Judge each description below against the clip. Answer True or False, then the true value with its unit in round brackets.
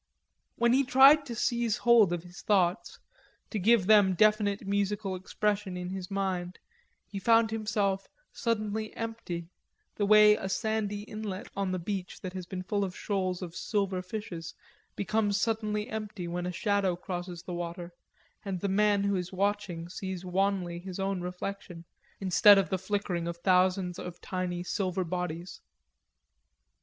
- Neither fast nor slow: True (155 wpm)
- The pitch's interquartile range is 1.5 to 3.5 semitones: True (2.7 semitones)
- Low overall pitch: False (195 Hz)